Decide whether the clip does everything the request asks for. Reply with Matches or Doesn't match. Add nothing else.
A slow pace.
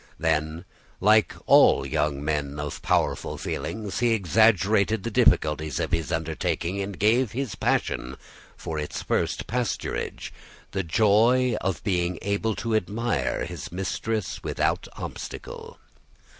Matches